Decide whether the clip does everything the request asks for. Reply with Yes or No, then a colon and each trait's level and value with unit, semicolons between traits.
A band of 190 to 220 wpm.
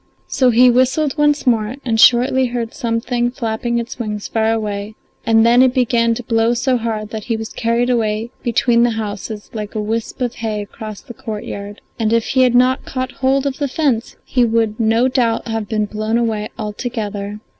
Yes: average, 195 wpm